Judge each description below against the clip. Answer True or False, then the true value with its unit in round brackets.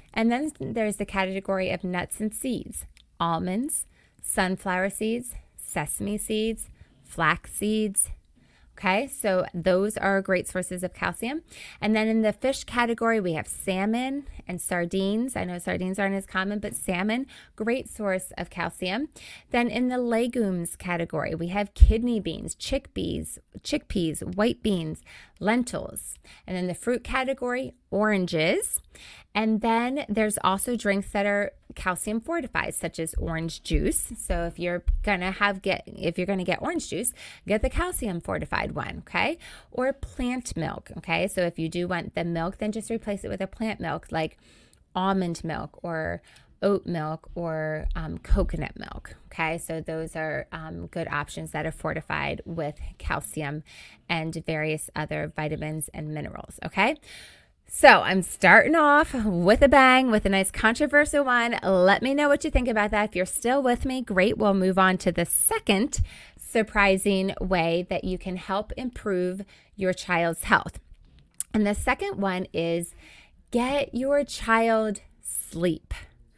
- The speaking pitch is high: True (195 Hz)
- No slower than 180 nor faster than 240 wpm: False (155 wpm)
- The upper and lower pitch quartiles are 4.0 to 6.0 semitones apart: True (4.6 semitones)